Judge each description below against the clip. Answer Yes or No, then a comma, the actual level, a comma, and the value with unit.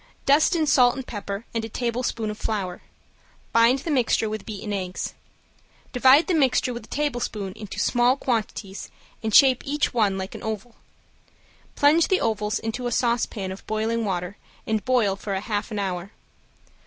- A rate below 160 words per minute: No, average, 170 wpm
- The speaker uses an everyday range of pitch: Yes, average, 3.7 semitones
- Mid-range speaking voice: No, high, 225 Hz